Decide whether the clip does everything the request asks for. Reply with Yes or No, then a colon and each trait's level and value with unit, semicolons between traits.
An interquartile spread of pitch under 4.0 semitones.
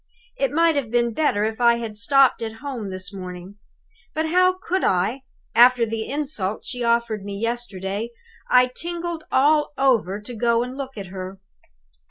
No: average, 4.9 semitones